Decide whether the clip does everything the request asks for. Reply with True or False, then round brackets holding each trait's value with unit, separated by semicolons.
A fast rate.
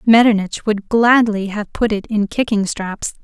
False (165 wpm)